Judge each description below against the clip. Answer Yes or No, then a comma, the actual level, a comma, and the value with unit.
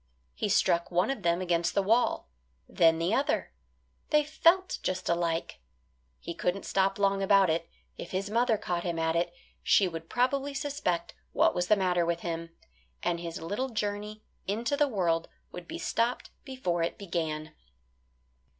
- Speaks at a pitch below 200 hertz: Yes, medium, 185 Hz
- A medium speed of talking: Yes, average, 165 wpm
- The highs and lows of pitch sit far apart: No, average, 4.6 semitones